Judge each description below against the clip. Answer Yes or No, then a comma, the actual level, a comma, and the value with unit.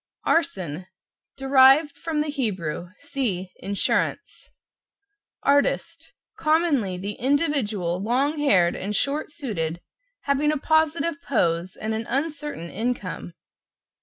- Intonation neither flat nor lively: No, wide, 7.8 semitones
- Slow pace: Yes, slow, 105 wpm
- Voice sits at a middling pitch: No, very high, 265 Hz